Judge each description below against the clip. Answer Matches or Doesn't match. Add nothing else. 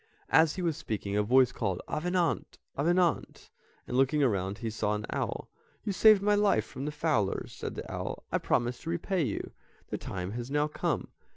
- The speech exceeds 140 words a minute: Matches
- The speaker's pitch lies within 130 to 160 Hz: Matches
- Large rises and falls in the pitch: Matches